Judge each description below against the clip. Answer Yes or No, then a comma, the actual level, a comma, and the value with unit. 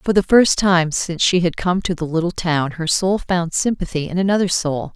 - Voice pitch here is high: No, medium, 175 Hz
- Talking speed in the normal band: No, fast, 230 wpm